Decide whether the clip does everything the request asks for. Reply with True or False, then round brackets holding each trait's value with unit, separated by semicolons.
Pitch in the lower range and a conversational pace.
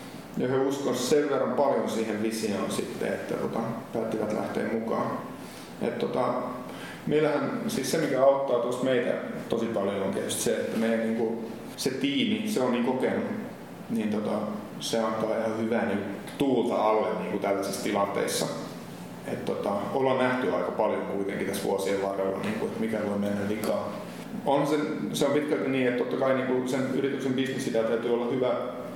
False (120 Hz; 160 wpm)